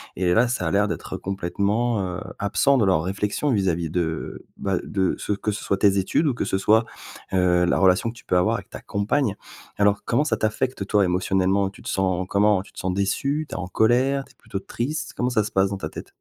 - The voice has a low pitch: Yes, low, 100 Hz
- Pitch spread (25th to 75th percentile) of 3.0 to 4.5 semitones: Yes, average, 3.4 semitones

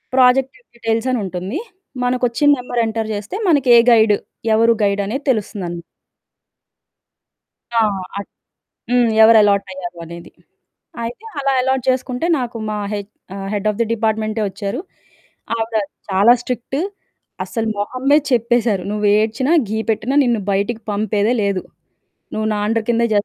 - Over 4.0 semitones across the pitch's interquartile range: No, average, 3.3 semitones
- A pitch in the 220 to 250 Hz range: Yes, high, 225 Hz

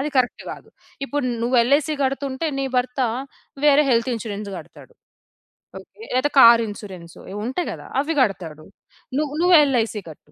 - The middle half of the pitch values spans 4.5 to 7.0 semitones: Yes, average, 5.1 semitones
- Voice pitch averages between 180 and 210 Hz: No, very high, 250 Hz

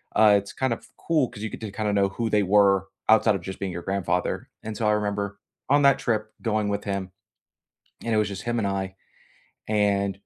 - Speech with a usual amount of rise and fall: No, narrow, 1.9 semitones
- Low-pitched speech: Yes, low, 105 Hz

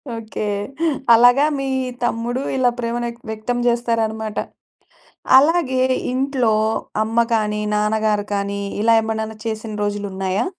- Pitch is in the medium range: No, high, 225 Hz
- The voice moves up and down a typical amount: No, narrow, 2.2 semitones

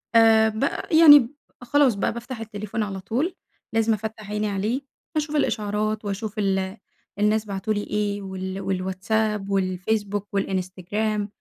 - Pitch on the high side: Yes, high, 210 Hz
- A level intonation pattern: Yes, narrow, 2.2 semitones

